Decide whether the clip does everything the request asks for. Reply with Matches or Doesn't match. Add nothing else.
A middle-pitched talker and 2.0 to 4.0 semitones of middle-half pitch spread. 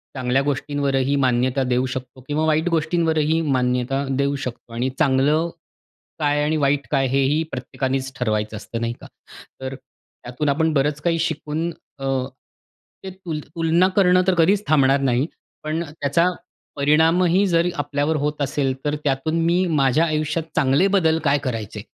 Matches